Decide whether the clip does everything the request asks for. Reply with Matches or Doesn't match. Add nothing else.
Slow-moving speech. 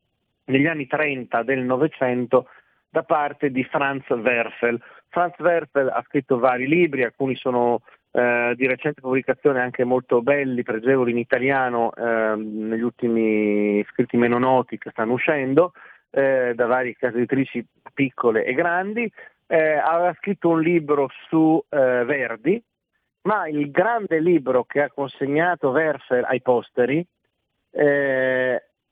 Doesn't match